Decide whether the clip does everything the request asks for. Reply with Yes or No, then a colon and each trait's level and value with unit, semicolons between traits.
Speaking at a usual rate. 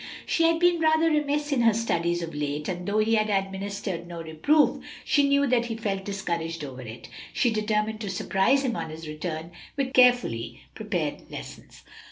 Yes: average, 185 wpm